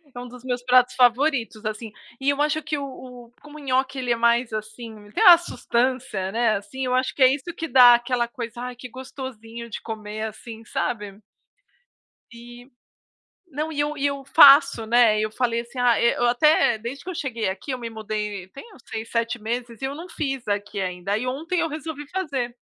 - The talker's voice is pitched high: Yes, high, 245 Hz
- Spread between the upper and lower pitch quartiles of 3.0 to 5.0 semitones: Yes, average, 3.4 semitones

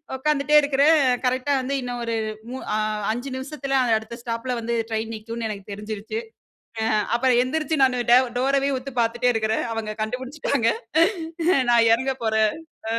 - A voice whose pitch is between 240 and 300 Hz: Yes, high, 245 Hz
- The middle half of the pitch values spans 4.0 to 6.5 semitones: No, average, 3.3 semitones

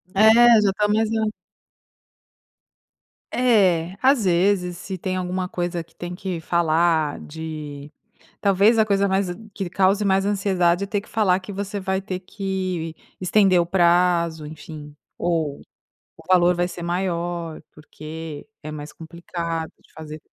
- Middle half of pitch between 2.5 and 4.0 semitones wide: Yes, average, 3.0 semitones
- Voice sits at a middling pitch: Yes, medium, 180 Hz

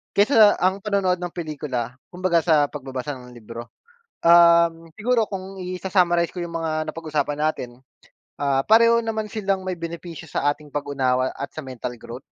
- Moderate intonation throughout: Yes, average, 4.5 semitones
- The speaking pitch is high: No, medium, 170 Hz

